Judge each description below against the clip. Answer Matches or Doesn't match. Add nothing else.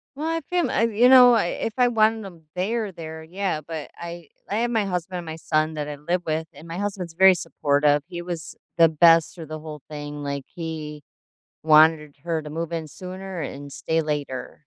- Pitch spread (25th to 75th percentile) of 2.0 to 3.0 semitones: Doesn't match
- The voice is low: Doesn't match